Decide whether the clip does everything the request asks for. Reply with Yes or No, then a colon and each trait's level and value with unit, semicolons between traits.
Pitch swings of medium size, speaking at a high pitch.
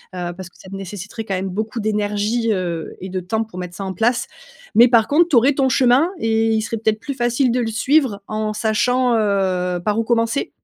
Yes: average, 3.6 semitones; high, 220 Hz